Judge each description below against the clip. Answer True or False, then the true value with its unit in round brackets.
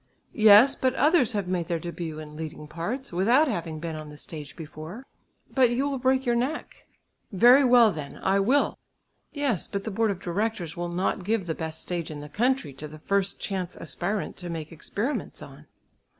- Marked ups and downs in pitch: True (6.8 semitones)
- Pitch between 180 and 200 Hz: True (190 Hz)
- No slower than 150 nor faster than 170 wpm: False (195 wpm)